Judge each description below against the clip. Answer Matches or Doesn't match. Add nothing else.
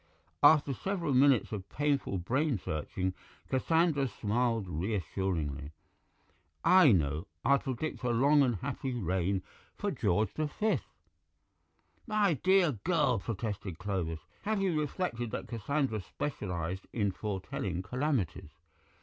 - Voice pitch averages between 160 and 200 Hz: Doesn't match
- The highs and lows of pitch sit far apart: Matches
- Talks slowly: Matches